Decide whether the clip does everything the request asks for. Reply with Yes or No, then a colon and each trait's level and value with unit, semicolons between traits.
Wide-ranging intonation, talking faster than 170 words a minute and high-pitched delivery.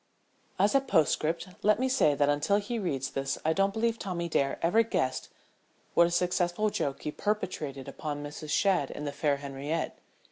No: wide, 5.7 semitones; average, 180 wpm; medium, 170 Hz